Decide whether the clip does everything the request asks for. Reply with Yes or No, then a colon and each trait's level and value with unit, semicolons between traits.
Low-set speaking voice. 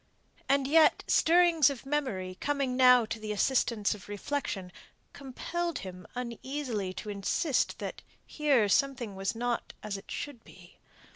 No: very high, 250 Hz